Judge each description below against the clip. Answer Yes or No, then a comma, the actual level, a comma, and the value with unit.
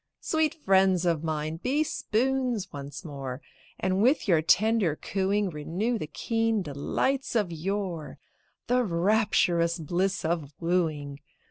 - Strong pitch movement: Yes, wide, 5.7 semitones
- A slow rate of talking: Yes, slow, 125 wpm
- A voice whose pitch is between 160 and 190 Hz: Yes, medium, 185 Hz